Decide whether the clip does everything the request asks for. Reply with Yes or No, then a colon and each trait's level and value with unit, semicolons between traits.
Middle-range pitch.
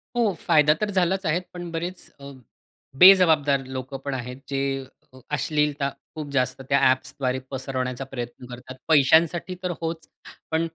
Yes: medium, 145 Hz